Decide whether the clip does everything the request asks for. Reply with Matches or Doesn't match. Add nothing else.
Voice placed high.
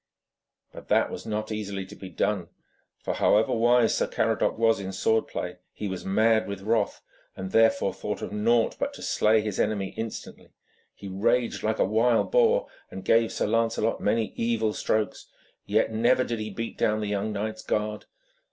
Doesn't match